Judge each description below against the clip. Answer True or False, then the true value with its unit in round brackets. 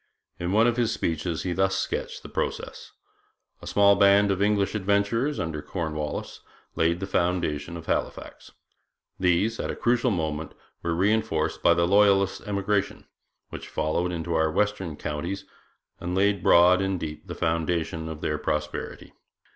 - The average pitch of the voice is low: True (90 Hz)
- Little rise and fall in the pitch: False (3.8 semitones)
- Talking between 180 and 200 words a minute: False (155 wpm)